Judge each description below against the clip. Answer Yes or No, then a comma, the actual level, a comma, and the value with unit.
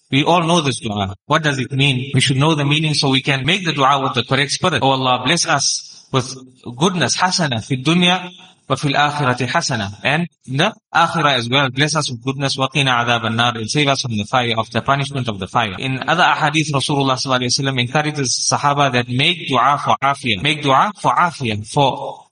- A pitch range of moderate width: Yes, average, 3.2 semitones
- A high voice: No, low, 135 Hz